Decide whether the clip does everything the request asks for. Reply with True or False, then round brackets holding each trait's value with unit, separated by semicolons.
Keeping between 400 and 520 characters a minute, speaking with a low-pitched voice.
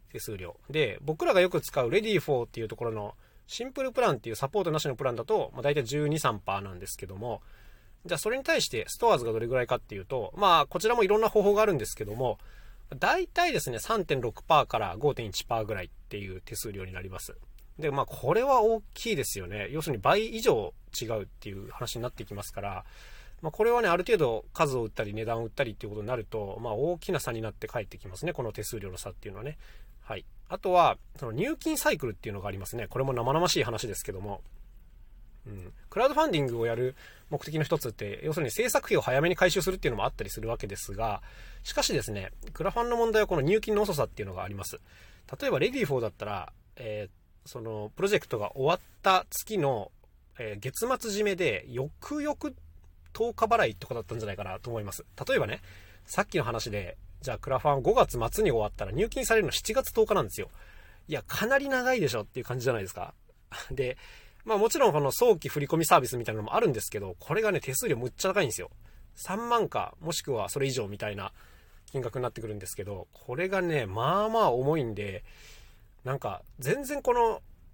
True (440 characters per minute; 120 Hz)